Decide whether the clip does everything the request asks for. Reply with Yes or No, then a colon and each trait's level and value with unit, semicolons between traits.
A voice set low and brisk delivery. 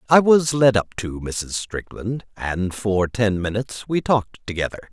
No: low, 110 Hz; average, 170 wpm